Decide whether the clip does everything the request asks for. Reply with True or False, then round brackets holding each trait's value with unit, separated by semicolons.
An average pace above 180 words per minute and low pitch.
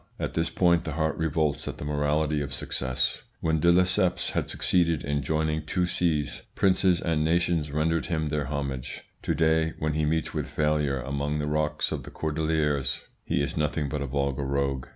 True (190 wpm; 75 Hz)